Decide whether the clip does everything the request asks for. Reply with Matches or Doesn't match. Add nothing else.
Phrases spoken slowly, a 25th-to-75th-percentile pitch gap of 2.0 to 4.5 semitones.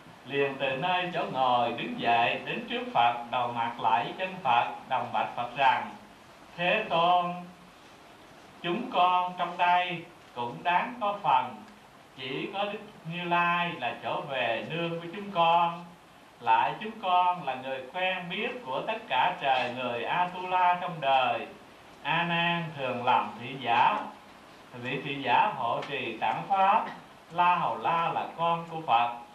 Doesn't match